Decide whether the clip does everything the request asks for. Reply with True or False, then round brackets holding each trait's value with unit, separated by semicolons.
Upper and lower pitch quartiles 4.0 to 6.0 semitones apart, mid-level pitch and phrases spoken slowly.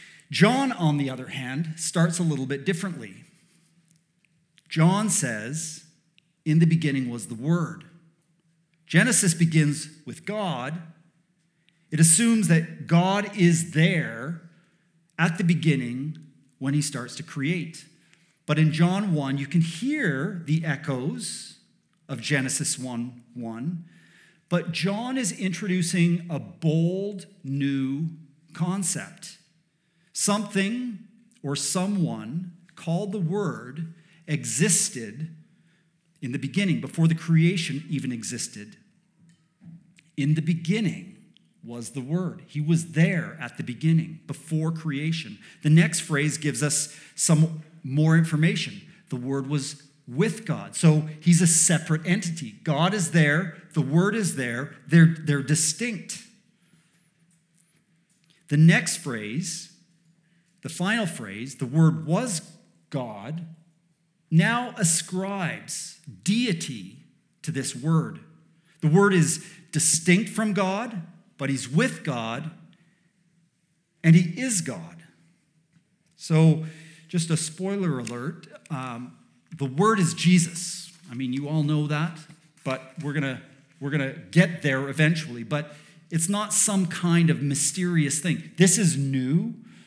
False (2.5 semitones; 165 Hz; 120 wpm)